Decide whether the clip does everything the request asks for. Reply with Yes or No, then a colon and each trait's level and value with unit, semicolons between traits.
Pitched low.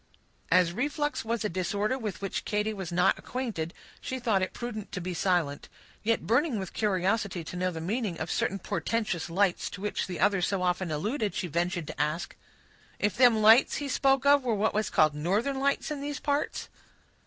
No: high, 205 Hz